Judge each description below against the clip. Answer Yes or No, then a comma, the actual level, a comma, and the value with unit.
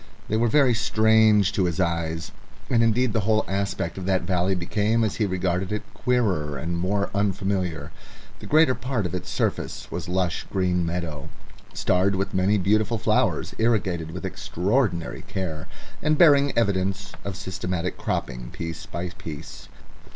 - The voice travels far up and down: No, average, 3.6 semitones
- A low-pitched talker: Yes, very low, 95 Hz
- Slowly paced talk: No, average, 155 wpm